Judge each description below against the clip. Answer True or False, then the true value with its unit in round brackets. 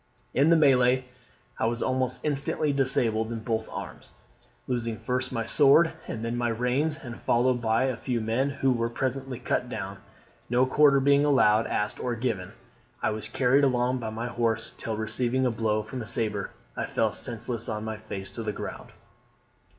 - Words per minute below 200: True (180 wpm)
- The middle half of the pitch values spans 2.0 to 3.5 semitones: True (2.8 semitones)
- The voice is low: True (120 Hz)